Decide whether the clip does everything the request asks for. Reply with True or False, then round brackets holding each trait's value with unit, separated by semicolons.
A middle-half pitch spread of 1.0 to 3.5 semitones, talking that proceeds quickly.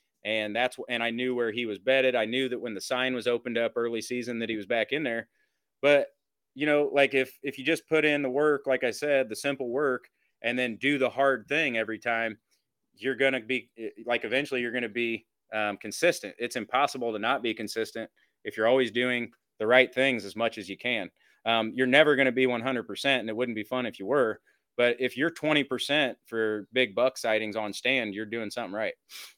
True (2.8 semitones; 225 wpm)